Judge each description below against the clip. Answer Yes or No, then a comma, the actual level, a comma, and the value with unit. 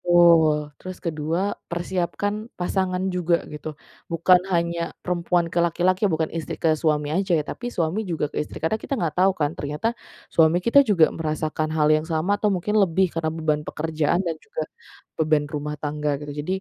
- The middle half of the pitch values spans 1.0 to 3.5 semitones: Yes, average, 3.0 semitones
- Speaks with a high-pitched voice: No, medium, 165 Hz